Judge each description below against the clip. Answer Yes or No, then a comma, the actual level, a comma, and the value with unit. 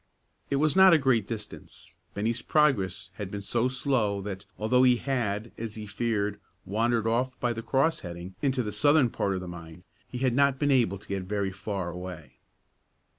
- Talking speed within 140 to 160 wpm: No, average, 190 wpm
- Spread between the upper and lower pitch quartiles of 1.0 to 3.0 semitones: No, average, 4.6 semitones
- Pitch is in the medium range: No, low, 110 Hz